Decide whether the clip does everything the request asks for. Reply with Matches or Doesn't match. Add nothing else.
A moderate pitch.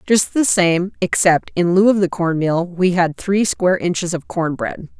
Matches